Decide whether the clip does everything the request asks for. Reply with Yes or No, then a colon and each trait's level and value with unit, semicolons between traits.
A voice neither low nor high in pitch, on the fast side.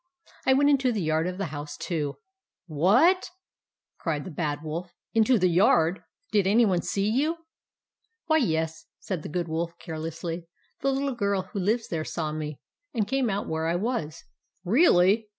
Yes: medium, 180 Hz; fast, 210 wpm